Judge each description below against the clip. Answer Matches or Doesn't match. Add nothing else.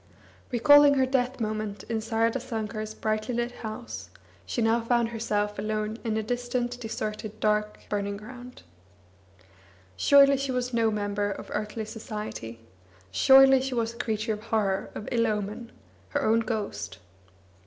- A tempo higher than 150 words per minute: Doesn't match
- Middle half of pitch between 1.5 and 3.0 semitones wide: Matches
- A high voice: Matches